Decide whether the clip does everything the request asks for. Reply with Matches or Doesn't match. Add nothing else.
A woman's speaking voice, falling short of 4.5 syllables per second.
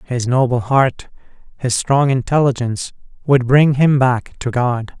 Doesn't match